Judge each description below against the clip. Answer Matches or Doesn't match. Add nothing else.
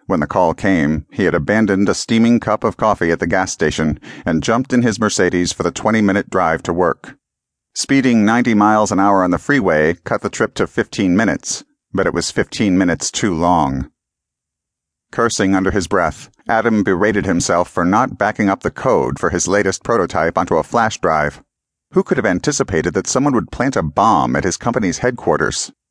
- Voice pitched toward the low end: Matches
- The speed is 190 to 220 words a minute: Matches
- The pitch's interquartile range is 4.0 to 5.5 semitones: Doesn't match